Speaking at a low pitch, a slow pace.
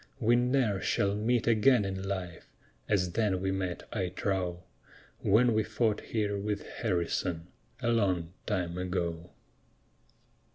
Yes: low, 100 Hz; slow, 130 wpm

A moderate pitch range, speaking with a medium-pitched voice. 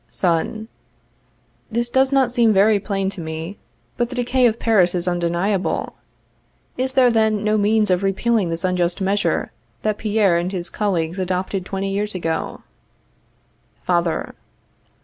No: average, 3.6 semitones; high, 200 Hz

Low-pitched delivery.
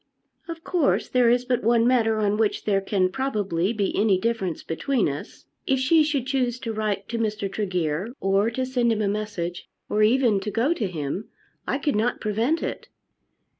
No: high, 220 Hz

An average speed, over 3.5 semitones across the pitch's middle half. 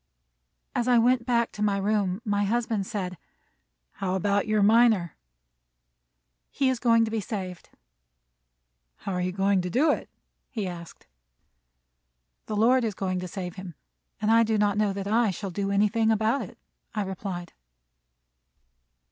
No: average, 155 wpm; average, 3.0 semitones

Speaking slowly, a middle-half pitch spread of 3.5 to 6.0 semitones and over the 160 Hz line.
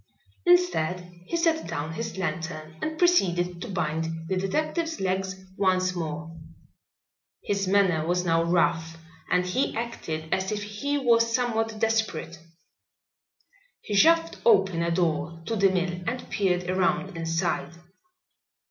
Yes: slow, 130 wpm; average, 4.8 semitones; medium, 185 Hz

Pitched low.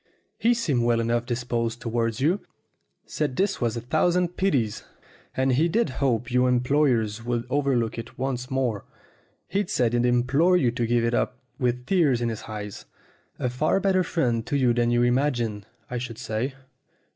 Yes: low, 125 Hz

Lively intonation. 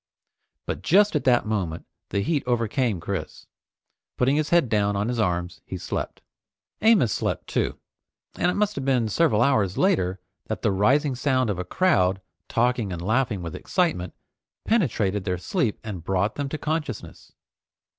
Yes: wide, 7.1 semitones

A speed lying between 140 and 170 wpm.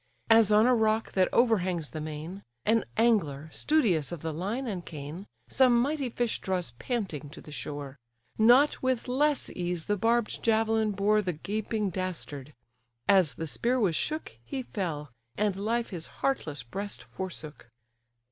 Yes: average, 155 wpm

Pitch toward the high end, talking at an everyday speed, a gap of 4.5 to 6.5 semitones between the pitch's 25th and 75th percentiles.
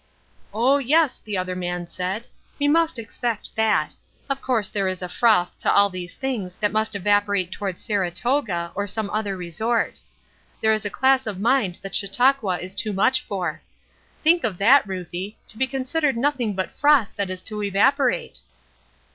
Yes: high, 210 Hz; average, 170 wpm; wide, 5.4 semitones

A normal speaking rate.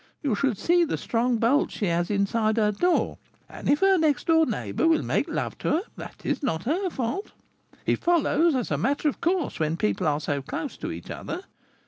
No: fast, 210 wpm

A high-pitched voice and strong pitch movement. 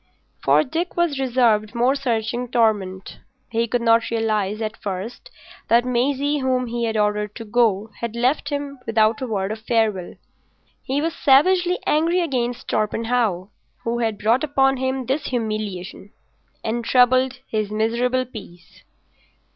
No: high, 235 Hz; average, 3.4 semitones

